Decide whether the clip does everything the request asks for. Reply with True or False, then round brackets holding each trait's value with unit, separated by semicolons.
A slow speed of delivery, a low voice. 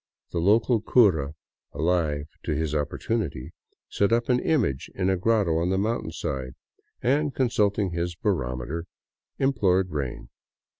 True (130 wpm; 90 Hz)